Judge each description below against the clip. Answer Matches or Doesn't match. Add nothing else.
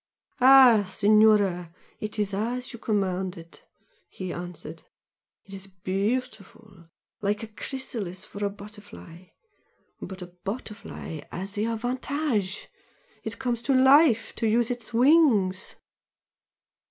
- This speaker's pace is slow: Matches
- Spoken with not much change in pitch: Doesn't match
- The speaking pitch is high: Matches